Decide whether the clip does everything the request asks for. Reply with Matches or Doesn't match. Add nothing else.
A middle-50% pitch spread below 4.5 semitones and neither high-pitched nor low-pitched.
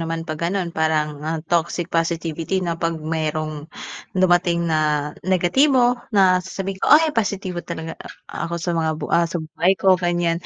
Matches